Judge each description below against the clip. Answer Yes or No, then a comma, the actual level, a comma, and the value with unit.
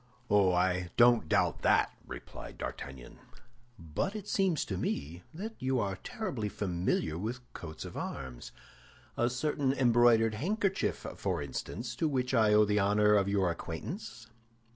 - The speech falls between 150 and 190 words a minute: No, average, 140 wpm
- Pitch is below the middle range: Yes, low, 110 Hz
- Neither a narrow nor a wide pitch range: No, wide, 6.1 semitones